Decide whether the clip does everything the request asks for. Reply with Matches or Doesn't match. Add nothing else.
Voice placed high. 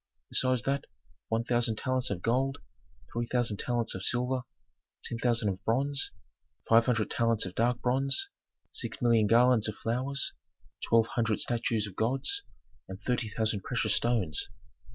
Doesn't match